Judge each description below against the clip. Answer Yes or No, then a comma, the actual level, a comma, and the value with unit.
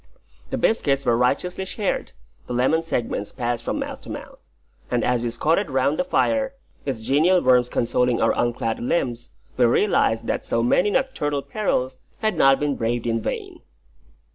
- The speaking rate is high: No, average, 165 wpm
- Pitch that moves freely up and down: Yes, wide, 5.7 semitones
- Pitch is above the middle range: No, low, 130 Hz